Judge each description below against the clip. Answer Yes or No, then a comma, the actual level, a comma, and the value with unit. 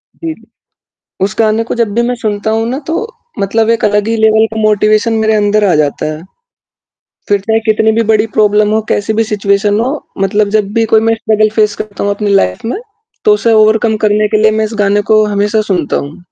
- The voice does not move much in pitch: Yes, narrow, 1.4 semitones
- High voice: Yes, high, 215 Hz